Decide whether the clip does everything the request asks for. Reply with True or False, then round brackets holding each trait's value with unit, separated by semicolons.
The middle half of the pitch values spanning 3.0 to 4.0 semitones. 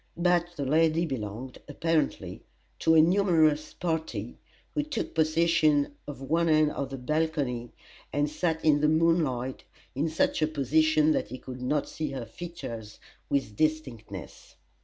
True (3.5 semitones)